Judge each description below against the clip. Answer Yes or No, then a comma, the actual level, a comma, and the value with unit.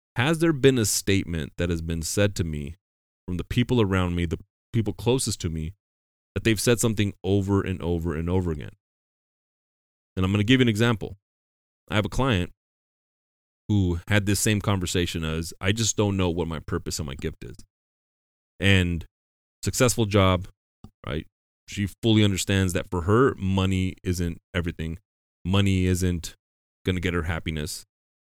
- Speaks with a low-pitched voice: Yes, very low, 95 Hz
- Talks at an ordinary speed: Yes, average, 170 wpm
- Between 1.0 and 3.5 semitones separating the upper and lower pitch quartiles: No, average, 4.1 semitones